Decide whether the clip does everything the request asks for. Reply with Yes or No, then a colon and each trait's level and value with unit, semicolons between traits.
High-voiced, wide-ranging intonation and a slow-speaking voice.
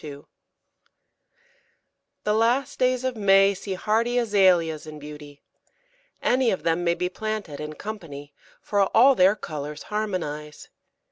Yes: high, 195 Hz; wide, 6.2 semitones; slow, 130 wpm